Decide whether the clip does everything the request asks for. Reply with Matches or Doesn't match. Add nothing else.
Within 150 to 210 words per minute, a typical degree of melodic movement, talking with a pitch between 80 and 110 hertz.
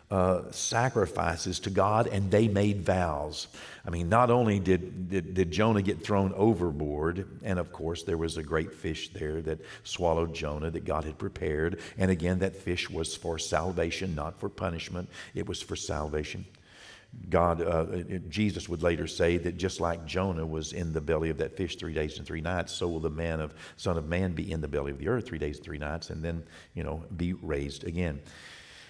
Matches